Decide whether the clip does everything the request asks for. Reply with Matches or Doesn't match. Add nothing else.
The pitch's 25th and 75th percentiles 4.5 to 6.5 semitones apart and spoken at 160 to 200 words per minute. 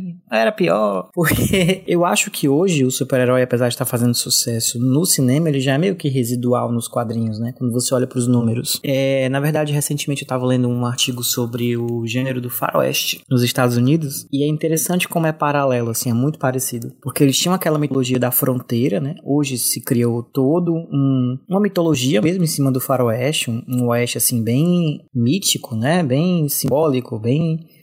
Doesn't match